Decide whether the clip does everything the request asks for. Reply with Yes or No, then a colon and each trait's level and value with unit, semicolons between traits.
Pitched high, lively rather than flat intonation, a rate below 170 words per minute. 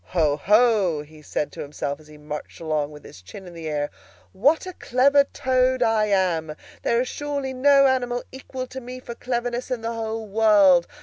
No: high, 225 Hz; wide, 8.1 semitones; average, 195 wpm